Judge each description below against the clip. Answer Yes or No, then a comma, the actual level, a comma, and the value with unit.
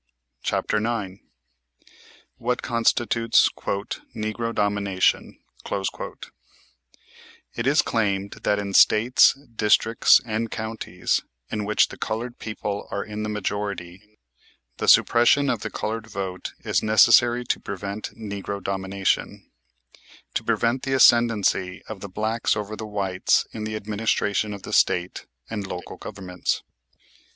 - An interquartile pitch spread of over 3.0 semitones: No, narrow, 2.5 semitones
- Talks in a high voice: No, low, 105 Hz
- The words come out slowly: Yes, slow, 120 wpm